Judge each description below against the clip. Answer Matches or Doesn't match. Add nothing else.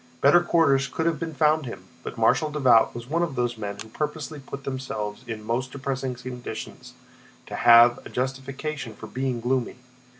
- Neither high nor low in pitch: Doesn't match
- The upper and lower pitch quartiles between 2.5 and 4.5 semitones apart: Matches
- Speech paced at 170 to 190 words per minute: Matches